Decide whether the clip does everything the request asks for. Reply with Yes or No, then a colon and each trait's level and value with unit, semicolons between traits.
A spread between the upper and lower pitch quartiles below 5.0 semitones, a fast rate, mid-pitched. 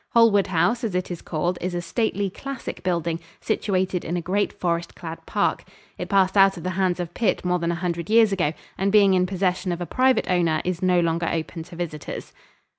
Yes: narrow, 2.4 semitones; fast, 215 wpm; medium, 180 Hz